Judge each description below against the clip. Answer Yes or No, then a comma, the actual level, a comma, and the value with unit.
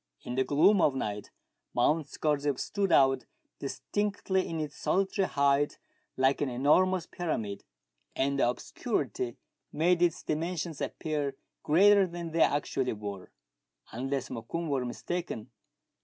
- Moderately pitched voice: Yes, medium, 145 Hz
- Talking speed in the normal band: No, slow, 125 wpm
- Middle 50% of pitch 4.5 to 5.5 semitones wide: Yes, average, 4.8 semitones